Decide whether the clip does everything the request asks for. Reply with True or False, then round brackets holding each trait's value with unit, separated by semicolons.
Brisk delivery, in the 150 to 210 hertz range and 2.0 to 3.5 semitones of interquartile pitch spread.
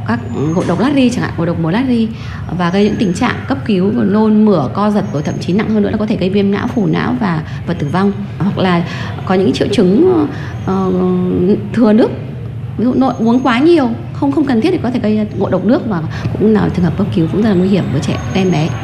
False (265 wpm; 190 Hz; 4.8 semitones)